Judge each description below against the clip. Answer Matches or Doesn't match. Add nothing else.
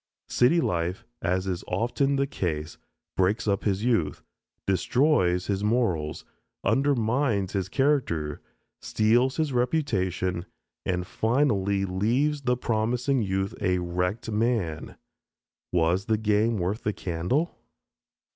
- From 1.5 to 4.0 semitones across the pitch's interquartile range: Doesn't match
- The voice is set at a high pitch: Doesn't match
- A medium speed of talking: Doesn't match